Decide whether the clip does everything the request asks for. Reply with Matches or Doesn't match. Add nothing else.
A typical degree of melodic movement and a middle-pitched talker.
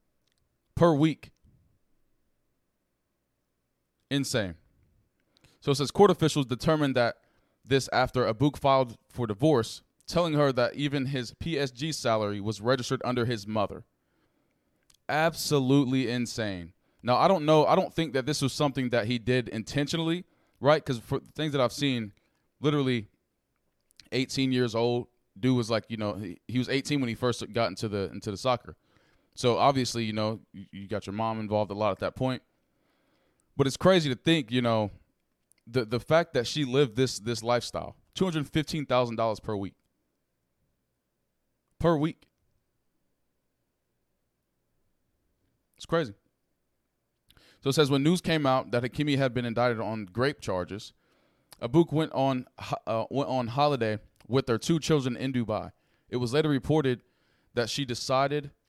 Doesn't match